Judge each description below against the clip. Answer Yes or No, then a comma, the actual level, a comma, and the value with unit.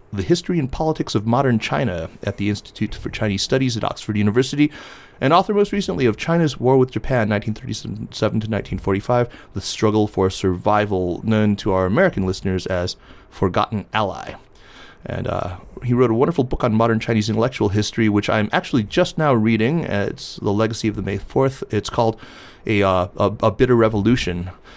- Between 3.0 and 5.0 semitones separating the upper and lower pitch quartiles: Yes, average, 3.7 semitones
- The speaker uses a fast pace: No, average, 175 wpm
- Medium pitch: No, low, 110 Hz